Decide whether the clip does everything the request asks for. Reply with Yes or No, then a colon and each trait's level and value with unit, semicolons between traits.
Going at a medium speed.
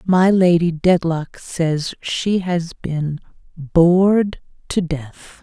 No: slow, 110 wpm